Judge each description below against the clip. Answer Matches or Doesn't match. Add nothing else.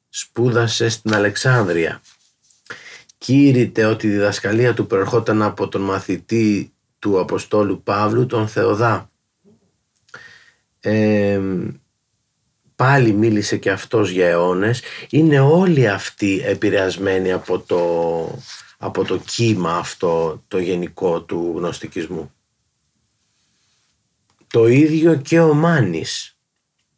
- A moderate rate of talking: Doesn't match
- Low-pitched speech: Matches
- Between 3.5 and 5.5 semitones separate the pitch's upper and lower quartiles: Matches